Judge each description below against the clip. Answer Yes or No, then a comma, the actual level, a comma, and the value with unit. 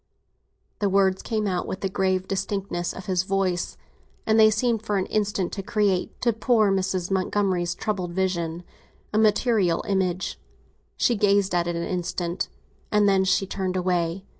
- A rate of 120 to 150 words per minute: No, average, 165 wpm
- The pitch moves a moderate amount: No, narrow, 2.2 semitones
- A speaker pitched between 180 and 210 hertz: Yes, high, 190 Hz